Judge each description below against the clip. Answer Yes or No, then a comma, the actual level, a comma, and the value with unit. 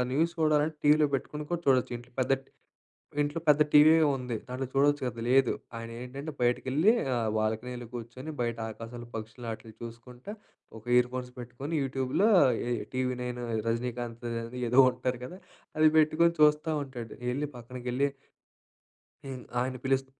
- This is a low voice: Yes, low, 125 Hz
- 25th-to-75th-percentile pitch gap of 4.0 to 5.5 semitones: No, average, 3.4 semitones